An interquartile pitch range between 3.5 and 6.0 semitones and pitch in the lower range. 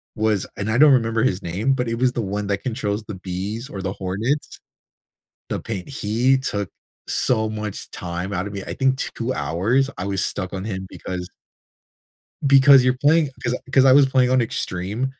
Yes: average, 4.9 semitones; low, 110 Hz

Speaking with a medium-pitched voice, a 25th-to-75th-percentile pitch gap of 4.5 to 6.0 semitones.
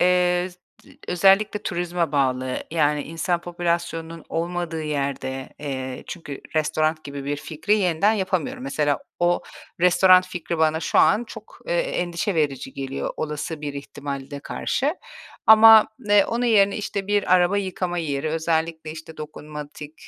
No: medium, 165 Hz; average, 3.7 semitones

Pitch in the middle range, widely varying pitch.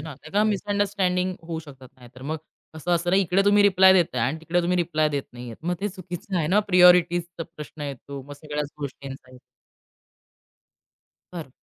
No: medium, 170 Hz; average, 4.2 semitones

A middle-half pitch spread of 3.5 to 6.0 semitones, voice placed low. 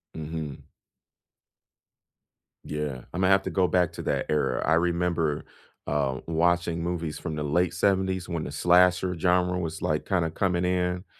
No: narrow, 2.4 semitones; very low, 85 Hz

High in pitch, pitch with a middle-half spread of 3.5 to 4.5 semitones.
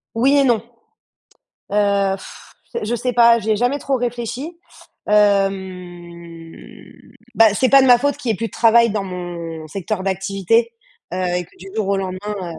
Yes: high, 205 Hz; average, 4.2 semitones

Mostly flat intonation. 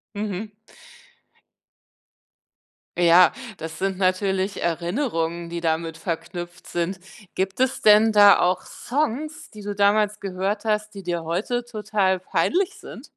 No: average, 3.5 semitones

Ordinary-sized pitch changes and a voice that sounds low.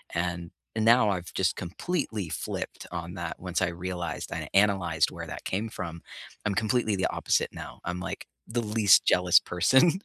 Yes: average, 3.8 semitones; very low, 95 Hz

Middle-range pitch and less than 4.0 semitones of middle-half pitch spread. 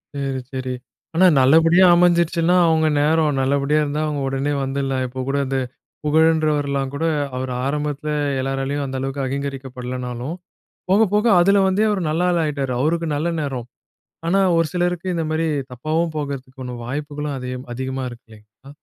Yes: medium, 145 Hz; average, 3.5 semitones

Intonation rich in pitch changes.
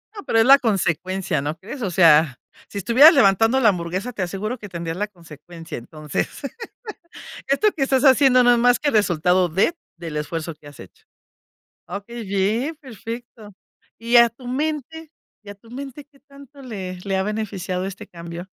Yes: wide, 6.2 semitones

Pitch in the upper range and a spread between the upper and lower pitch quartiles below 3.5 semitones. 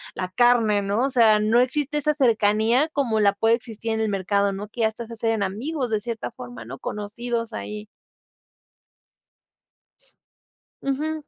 Yes: high, 225 Hz; average, 2.9 semitones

